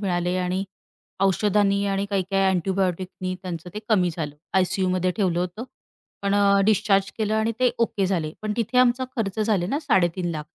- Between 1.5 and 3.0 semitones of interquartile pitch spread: Yes, narrow, 2.6 semitones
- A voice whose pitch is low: No, high, 195 Hz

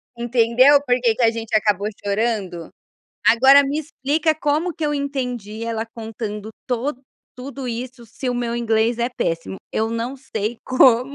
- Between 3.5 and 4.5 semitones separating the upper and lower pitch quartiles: No, average, 3.1 semitones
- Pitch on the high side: Yes, high, 240 Hz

